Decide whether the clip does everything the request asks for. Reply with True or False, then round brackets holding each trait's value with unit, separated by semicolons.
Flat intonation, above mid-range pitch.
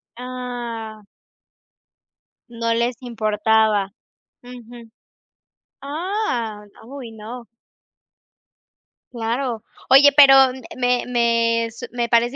True (1.9 semitones; 235 Hz)